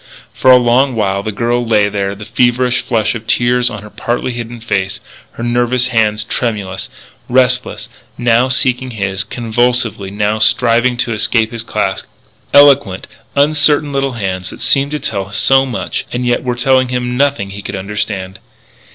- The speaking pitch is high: No, low, 120 Hz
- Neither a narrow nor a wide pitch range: Yes, average, 3.2 semitones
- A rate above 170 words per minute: No, average, 165 wpm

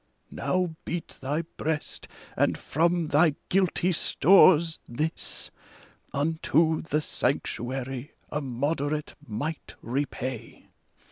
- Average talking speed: No, slow, 90 wpm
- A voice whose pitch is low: No, medium, 150 Hz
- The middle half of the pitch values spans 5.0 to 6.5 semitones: No, average, 3.5 semitones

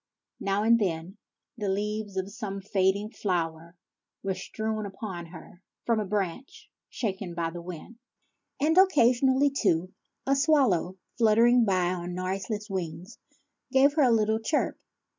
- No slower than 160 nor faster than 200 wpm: No, average, 140 wpm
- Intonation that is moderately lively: Yes, average, 4.1 semitones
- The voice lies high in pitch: Yes, high, 205 Hz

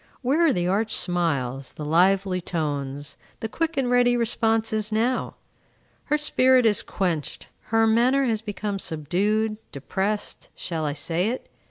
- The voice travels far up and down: Yes, wide, 5.7 semitones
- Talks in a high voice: Yes, high, 210 Hz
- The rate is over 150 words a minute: No, average, 145 wpm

